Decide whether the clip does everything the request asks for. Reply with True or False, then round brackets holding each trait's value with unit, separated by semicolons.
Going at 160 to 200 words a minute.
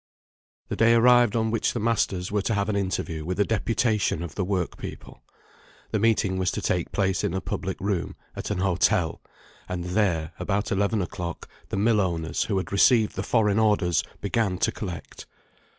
True (185 wpm)